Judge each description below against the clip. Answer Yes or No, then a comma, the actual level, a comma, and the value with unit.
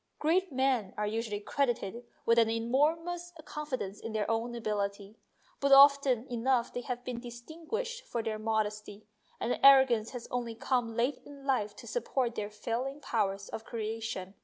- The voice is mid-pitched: No, high, 235 Hz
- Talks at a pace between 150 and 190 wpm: Yes, average, 160 wpm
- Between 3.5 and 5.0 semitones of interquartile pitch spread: Yes, average, 3.9 semitones